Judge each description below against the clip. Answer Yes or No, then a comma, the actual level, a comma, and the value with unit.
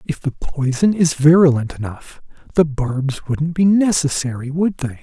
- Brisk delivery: No, average, 155 wpm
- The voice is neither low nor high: Yes, medium, 150 Hz